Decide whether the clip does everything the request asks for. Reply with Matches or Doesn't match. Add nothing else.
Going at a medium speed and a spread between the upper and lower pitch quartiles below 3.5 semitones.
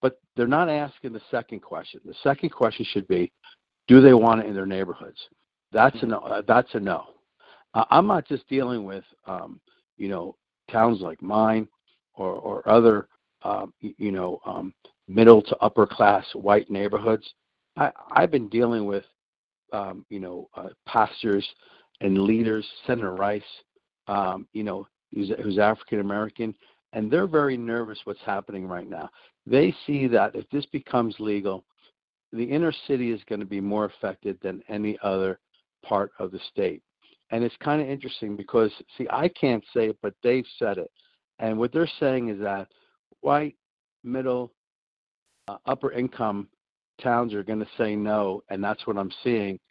Doesn't match